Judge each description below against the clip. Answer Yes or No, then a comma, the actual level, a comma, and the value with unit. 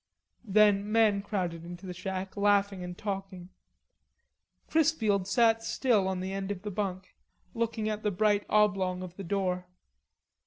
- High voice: Yes, high, 200 Hz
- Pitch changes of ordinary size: No, narrow, 2.3 semitones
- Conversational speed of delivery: Yes, average, 150 wpm